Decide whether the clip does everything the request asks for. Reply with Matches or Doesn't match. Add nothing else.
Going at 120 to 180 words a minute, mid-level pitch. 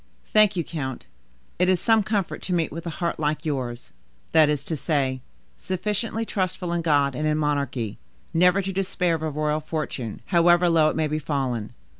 Doesn't match